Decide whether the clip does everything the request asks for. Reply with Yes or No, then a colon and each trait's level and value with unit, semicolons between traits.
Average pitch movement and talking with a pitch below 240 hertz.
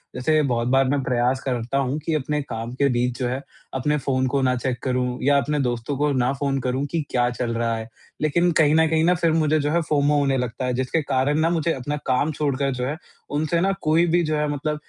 Yes: average, 3.2 semitones; medium, 140 Hz